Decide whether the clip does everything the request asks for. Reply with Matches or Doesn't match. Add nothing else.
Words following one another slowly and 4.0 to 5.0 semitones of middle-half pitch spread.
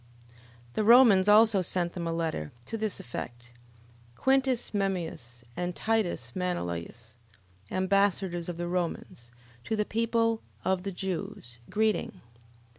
Matches